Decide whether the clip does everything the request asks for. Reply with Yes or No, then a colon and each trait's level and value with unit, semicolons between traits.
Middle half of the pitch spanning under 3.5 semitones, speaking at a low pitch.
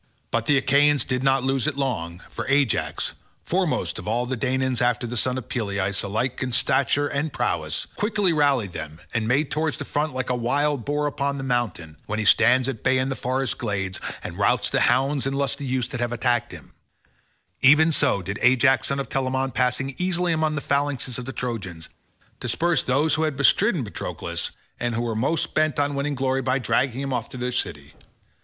Yes: average, 2.9 semitones; low, 130 Hz